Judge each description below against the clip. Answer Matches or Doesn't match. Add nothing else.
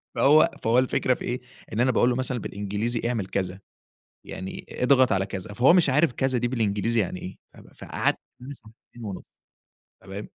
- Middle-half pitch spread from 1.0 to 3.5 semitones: Doesn't match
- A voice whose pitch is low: Matches